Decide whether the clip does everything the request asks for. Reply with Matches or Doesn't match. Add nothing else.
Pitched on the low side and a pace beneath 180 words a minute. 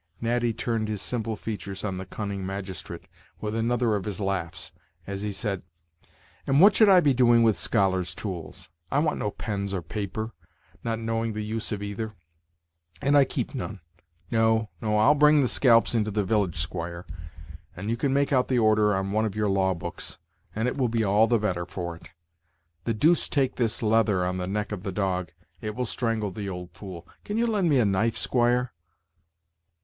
Doesn't match